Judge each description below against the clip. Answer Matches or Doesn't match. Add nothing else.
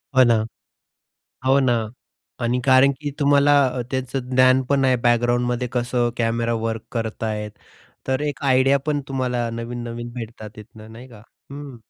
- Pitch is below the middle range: Matches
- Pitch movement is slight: Matches